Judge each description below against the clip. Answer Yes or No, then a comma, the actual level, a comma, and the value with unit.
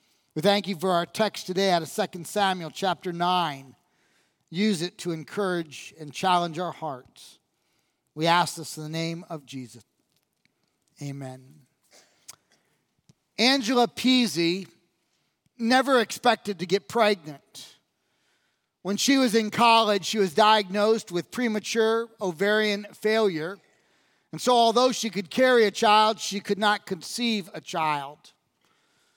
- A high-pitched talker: Yes, high, 195 Hz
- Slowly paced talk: Yes, slow, 130 wpm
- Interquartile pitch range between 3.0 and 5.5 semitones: Yes, average, 4.5 semitones